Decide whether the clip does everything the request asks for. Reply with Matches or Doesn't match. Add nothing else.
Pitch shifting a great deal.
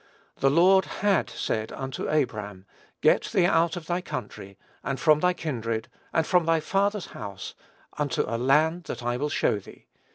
Matches